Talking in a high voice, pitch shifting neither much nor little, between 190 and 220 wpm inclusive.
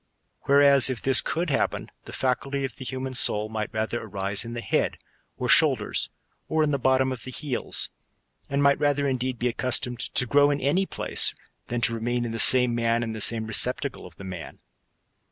No: low, 125 Hz; average, 3.2 semitones; average, 200 wpm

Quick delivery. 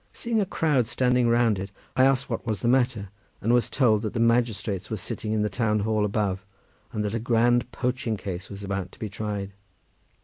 Yes: fast, 210 wpm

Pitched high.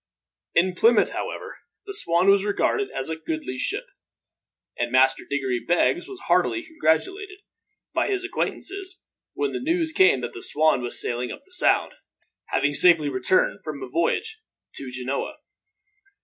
No: medium, 180 Hz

